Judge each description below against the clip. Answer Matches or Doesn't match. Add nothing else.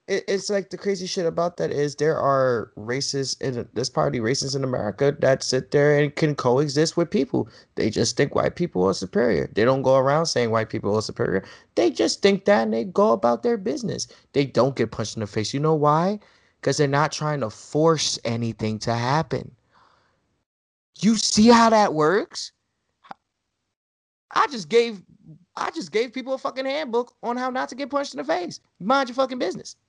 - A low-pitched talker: Doesn't match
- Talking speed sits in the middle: Matches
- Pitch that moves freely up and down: Matches